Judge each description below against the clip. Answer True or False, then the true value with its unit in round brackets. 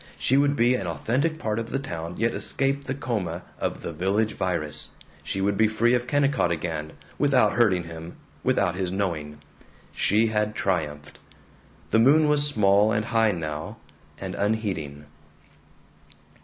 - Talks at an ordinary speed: True (155 wpm)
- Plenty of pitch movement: True (5.9 semitones)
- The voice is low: True (105 Hz)